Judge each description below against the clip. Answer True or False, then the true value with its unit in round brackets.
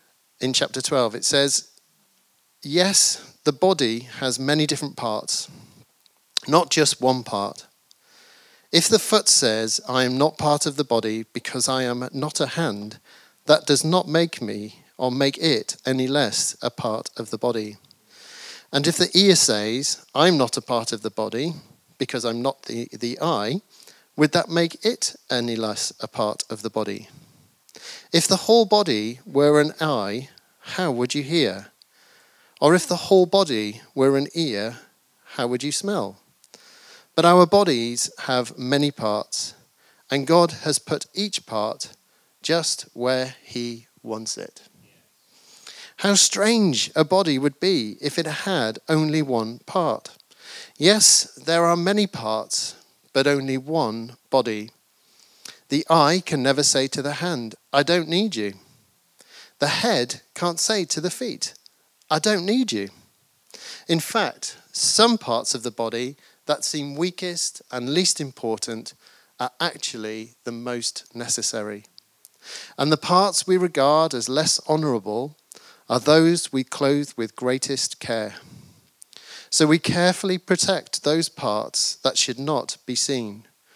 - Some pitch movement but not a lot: False (5.7 semitones)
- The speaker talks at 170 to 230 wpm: False (145 wpm)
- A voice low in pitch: False (145 Hz)